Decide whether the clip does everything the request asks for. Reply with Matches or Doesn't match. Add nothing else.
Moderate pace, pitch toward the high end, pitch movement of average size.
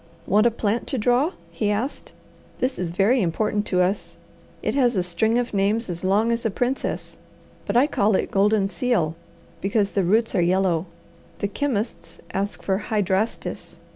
Matches